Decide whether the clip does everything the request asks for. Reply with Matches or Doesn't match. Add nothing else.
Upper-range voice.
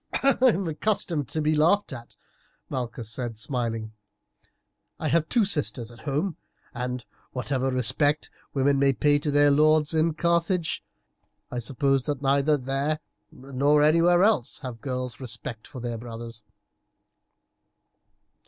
Doesn't match